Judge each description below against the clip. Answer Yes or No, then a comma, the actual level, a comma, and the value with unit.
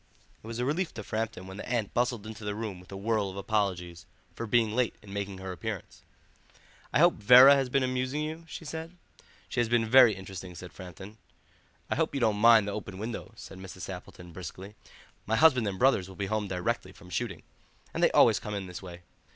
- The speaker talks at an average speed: No, fast, 215 wpm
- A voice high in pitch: No, low, 105 Hz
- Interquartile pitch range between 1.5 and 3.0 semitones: No, average, 4.3 semitones